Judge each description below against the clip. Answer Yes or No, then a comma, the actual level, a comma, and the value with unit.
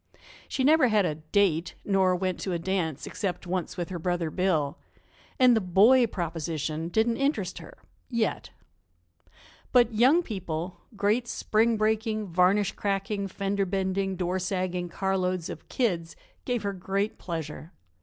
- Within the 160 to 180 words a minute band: No, average, 145 wpm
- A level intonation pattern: No, average, 3.5 semitones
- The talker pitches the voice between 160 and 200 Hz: Yes, high, 190 Hz